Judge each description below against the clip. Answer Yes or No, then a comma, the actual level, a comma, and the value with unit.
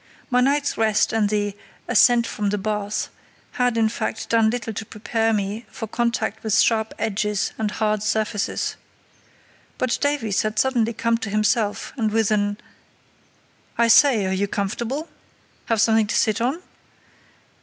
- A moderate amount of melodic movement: No, narrow, 1.9 semitones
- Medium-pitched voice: No, high, 220 Hz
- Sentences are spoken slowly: No, average, 155 wpm